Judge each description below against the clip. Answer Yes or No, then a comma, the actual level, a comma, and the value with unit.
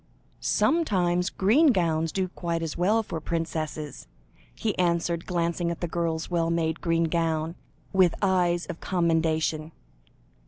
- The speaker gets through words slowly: Yes, slow, 130 wpm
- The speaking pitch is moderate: Yes, medium, 170 Hz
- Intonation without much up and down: Yes, narrow, 1.7 semitones